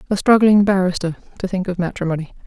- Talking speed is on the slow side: No, average, 170 wpm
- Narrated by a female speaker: Yes, female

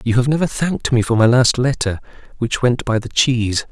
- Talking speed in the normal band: No, fast, 225 wpm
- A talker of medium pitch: No, low, 120 Hz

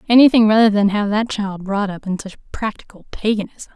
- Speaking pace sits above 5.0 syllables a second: Yes, 5.6 syllables/s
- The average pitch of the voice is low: No, high, 210 Hz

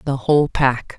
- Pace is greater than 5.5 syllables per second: No, 4.7 syllables/s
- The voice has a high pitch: No, low, 135 Hz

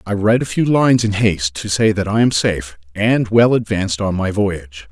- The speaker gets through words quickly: Yes, fast, 220 wpm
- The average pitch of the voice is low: Yes, low, 100 Hz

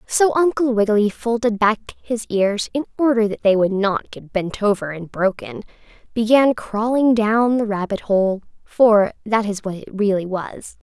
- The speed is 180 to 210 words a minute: No, average, 170 wpm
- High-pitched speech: Yes, high, 215 Hz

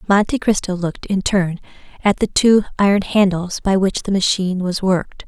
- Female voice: Yes, female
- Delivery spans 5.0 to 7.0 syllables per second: Yes, 5.3 syllables/s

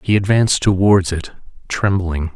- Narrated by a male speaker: Yes, male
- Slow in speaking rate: Yes, slow, 125 wpm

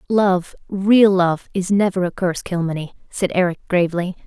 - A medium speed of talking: No, slow, 125 wpm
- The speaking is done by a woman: Yes, female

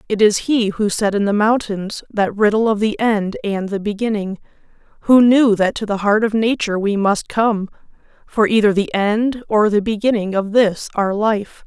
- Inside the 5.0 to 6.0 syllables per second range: No, 4.7 syllables/s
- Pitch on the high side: Yes, high, 210 Hz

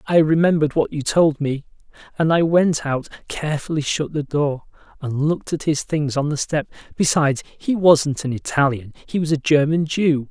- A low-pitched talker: No, medium, 150 Hz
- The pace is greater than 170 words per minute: Yes, average, 180 wpm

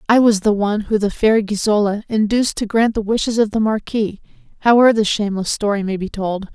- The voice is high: Yes, high, 210 Hz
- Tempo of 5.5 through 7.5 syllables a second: Yes, 6.0 syllables/s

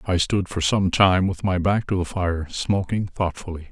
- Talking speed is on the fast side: Yes, fast, 210 wpm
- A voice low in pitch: Yes, very low, 90 Hz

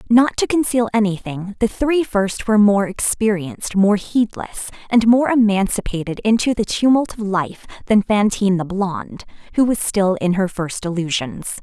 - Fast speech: No, average, 160 wpm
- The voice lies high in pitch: Yes, high, 205 Hz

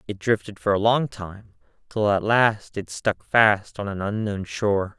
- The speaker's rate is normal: Yes, average, 190 wpm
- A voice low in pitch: Yes, low, 105 Hz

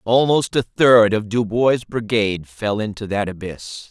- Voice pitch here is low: Yes, low, 110 Hz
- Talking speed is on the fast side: No, average, 155 wpm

